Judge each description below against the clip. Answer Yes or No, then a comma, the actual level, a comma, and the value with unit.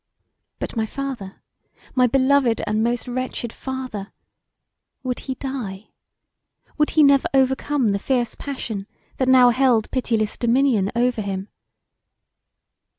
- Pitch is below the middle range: No, very high, 250 Hz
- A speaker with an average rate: No, slow, 120 wpm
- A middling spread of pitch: Yes, average, 3.3 semitones